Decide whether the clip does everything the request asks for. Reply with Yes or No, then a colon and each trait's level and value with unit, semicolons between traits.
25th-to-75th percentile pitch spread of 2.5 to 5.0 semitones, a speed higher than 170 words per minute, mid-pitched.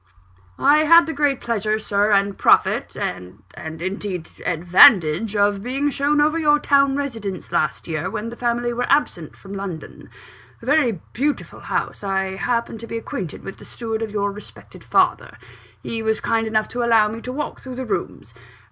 No: average, 4.7 semitones; average, 180 wpm; high, 220 Hz